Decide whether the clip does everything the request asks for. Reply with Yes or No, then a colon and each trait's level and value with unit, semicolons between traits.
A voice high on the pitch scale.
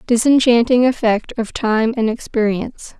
Yes: high, 235 Hz